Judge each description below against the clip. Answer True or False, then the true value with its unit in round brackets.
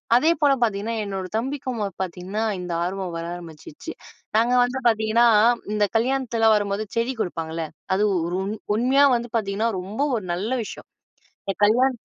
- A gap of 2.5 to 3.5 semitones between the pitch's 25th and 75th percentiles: False (4.0 semitones)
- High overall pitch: True (215 Hz)